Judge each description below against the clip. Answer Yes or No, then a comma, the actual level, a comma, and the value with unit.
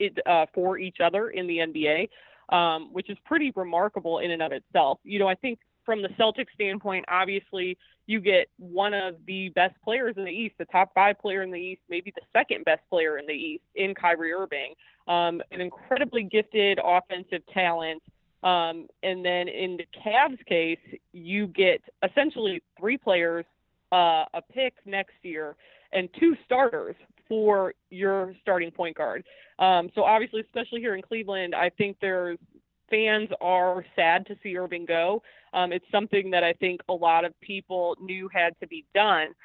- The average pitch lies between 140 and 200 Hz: Yes, medium, 185 Hz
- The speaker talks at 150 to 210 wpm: Yes, average, 180 wpm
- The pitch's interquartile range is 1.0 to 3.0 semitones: No, average, 3.4 semitones